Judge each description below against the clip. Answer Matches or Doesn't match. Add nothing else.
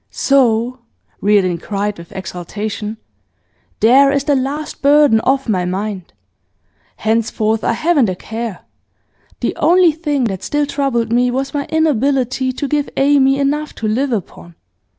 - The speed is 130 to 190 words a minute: Matches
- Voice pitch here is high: Matches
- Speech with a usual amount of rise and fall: Matches